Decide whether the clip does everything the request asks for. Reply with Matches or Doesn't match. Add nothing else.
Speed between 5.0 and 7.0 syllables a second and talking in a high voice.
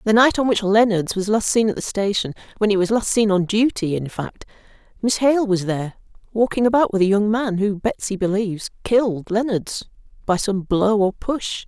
Matches